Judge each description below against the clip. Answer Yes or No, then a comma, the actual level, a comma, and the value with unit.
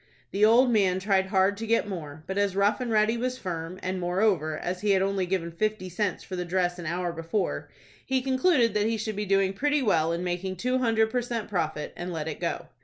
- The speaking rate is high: Yes, fast, 235 wpm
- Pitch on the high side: Yes, high, 195 Hz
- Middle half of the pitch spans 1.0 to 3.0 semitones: No, average, 3.7 semitones